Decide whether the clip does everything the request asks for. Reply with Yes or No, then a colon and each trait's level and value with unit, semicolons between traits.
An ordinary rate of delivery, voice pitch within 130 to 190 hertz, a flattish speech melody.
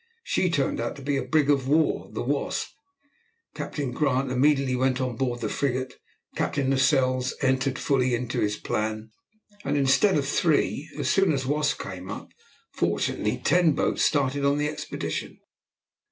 Yes: average, 165 wpm; low, 135 Hz; narrow, 2.3 semitones